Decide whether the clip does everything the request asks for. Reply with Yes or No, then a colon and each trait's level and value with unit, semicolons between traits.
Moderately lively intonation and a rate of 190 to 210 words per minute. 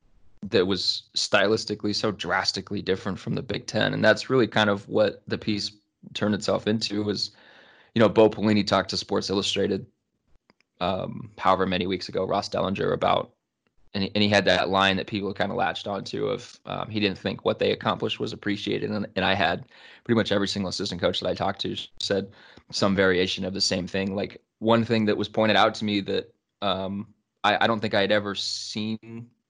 No: narrow, 1.9 semitones; fast, 205 wpm